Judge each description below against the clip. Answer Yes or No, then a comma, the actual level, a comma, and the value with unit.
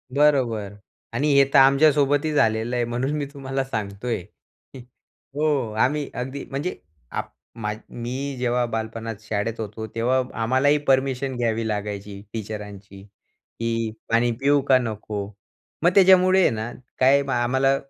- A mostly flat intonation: No, average, 3.8 semitones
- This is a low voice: Yes, low, 120 Hz